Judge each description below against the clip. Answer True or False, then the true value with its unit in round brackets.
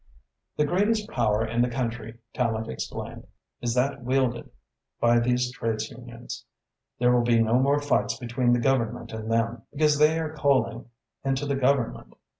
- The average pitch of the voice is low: True (120 Hz)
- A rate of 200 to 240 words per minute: False (160 wpm)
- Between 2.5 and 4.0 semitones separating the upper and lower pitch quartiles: True (2.8 semitones)